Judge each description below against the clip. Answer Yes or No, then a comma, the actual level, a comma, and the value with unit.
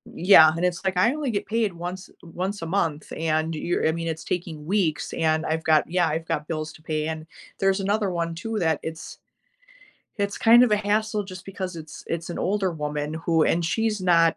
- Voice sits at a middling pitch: Yes, medium, 170 Hz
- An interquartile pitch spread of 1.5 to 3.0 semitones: No, average, 3.7 semitones